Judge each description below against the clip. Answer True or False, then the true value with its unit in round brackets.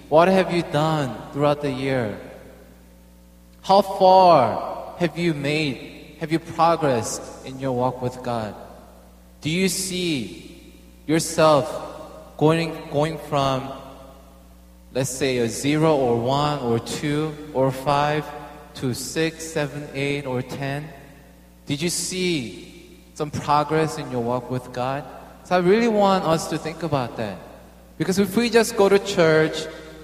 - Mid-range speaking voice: True (145 Hz)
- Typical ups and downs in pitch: True (4.3 semitones)